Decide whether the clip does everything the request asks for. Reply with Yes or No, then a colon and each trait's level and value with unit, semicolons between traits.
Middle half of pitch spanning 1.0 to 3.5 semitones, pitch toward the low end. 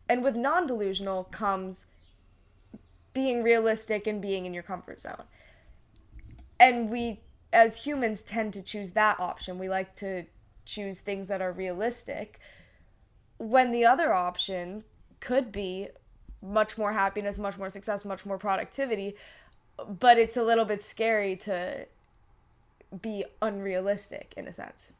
No: average, 2.9 semitones; high, 205 Hz